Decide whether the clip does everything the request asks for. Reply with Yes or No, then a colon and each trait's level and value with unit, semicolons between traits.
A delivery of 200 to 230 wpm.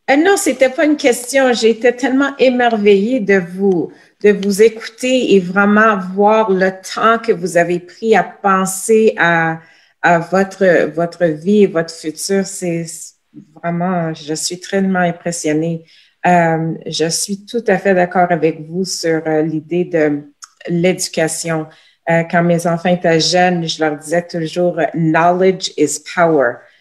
No: average, 150 wpm